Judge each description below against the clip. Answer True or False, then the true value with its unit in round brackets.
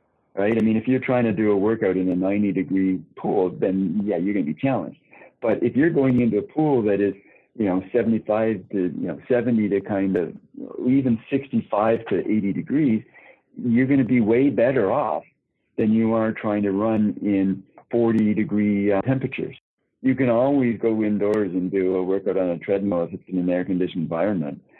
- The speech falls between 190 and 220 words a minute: True (200 wpm)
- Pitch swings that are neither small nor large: True (3.3 semitones)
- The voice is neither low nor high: False (105 Hz)